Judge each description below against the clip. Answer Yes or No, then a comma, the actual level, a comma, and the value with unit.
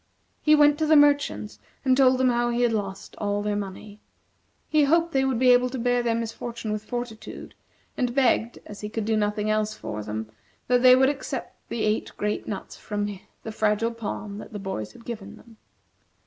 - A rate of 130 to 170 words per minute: No, fast, 205 wpm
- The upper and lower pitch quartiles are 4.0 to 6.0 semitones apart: No, average, 3.3 semitones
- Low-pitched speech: No, high, 225 Hz